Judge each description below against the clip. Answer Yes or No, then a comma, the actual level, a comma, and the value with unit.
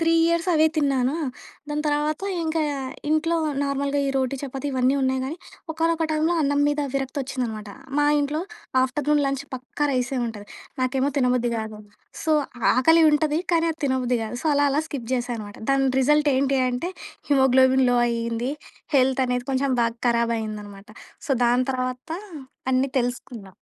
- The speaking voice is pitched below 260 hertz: No, very high, 265 Hz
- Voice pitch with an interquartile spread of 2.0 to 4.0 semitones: Yes, average, 3.1 semitones